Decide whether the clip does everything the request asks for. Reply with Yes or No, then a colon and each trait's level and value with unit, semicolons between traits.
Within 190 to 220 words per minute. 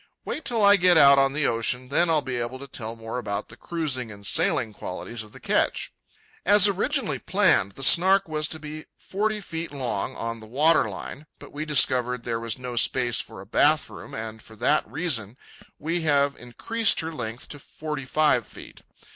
Yes: average, 195 wpm